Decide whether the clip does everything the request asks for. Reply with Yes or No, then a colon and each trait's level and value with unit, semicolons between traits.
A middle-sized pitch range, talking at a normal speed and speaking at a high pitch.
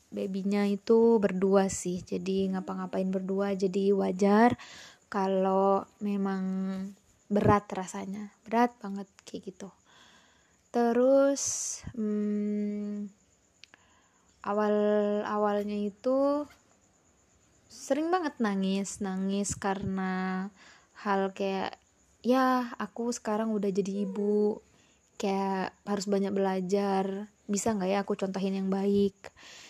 No: narrow, 1.3 semitones; average, 95 wpm; high, 200 Hz